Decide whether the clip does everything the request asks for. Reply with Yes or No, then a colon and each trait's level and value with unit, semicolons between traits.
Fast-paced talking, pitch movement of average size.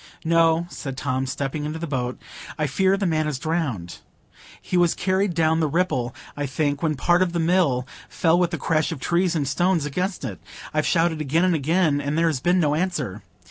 Yes: fast, 210 wpm; average, 3.5 semitones